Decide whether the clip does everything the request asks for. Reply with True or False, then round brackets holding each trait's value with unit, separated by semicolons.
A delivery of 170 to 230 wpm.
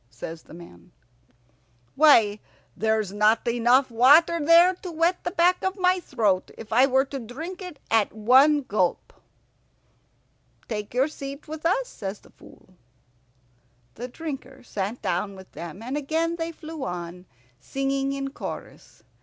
False (145 wpm)